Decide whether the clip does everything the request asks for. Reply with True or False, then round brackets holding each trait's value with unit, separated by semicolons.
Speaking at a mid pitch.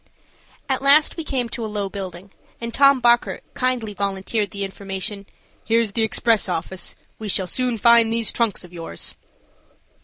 False (220 Hz)